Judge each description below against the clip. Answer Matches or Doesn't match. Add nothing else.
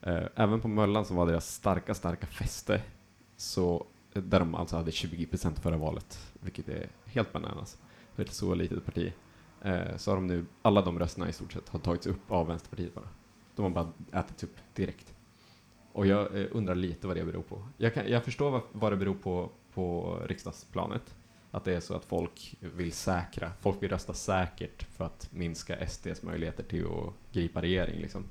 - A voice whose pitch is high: Doesn't match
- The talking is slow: Doesn't match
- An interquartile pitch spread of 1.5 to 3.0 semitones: Doesn't match